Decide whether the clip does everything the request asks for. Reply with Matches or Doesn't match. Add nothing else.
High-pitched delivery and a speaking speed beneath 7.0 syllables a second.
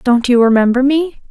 Matches